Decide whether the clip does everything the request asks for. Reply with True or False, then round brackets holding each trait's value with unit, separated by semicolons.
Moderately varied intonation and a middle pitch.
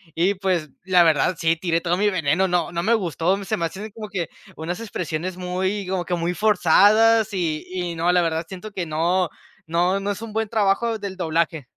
True (3.0 semitones; 180 Hz)